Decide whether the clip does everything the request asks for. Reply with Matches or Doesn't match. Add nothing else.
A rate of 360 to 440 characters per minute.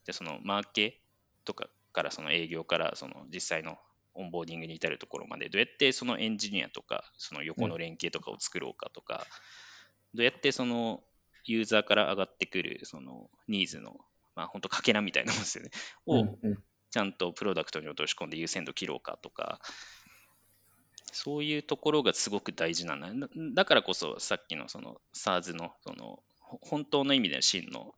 Matches